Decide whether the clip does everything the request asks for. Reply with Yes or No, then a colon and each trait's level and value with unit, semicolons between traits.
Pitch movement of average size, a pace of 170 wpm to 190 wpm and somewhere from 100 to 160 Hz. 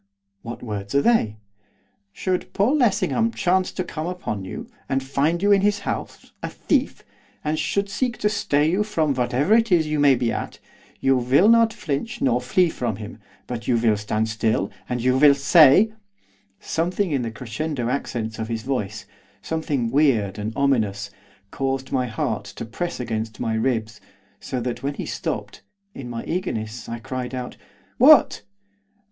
No: wide, 7.3 semitones; average, 175 wpm; low, 135 Hz